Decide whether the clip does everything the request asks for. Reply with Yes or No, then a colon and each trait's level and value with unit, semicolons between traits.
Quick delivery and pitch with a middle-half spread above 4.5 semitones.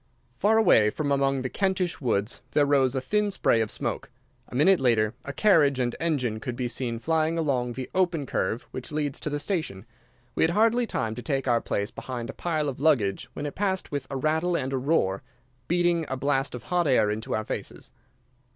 Yes: fast, 210 wpm; average, 5.2 semitones